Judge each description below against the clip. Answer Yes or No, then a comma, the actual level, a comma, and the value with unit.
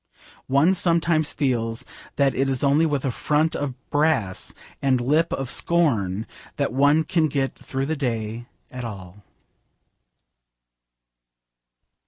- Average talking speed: No, slow, 130 wpm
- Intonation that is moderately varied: Yes, average, 4.4 semitones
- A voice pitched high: No, low, 135 Hz